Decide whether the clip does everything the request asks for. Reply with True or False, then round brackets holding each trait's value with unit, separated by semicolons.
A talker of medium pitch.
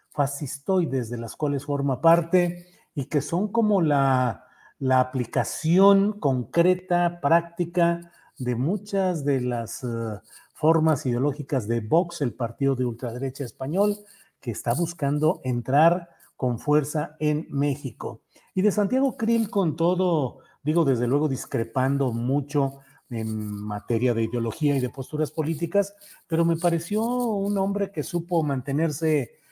True (145 Hz)